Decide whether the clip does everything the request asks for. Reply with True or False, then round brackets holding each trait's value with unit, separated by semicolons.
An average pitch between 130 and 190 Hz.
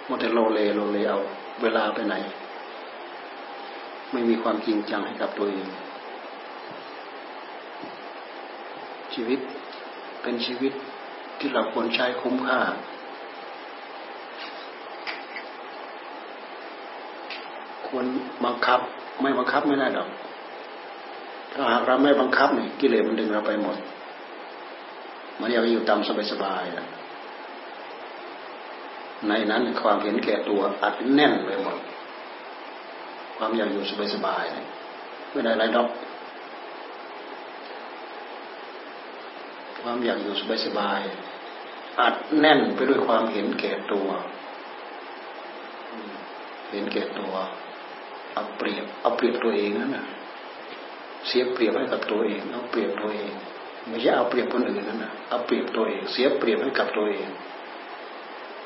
False (115 Hz)